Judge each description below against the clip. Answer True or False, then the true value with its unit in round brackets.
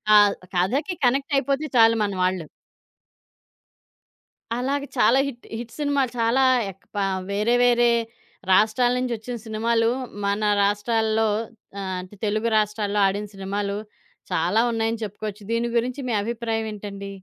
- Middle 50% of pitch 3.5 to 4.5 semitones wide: False (2.9 semitones)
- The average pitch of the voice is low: False (220 Hz)